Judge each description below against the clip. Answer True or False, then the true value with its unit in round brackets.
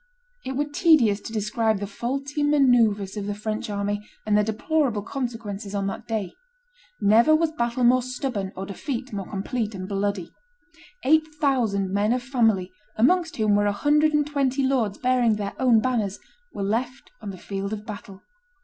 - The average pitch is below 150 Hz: False (220 Hz)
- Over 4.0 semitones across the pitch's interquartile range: True (4.5 semitones)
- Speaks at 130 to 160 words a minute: False (175 wpm)